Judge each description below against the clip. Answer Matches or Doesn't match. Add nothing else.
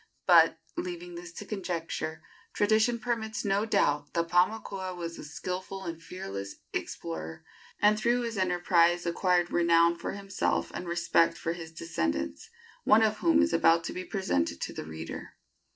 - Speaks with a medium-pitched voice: Matches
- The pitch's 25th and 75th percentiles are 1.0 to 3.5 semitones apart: Doesn't match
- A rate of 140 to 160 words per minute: Matches